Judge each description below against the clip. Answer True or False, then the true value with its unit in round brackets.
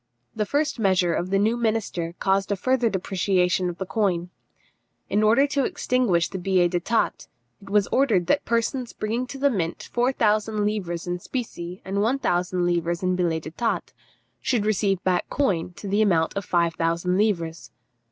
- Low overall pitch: False (195 Hz)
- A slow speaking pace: False (175 wpm)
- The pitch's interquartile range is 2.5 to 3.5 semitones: False (4.2 semitones)